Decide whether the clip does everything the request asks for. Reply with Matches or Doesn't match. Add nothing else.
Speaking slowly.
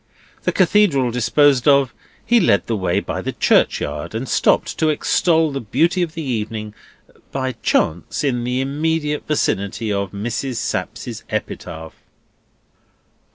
Matches